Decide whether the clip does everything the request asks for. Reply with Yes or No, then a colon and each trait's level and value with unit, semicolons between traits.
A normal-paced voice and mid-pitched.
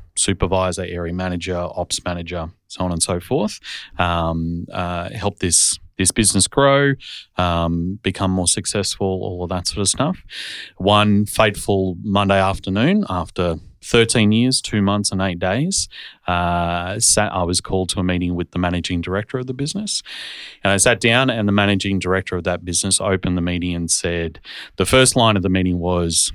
No: average, 175 wpm; very low, 95 Hz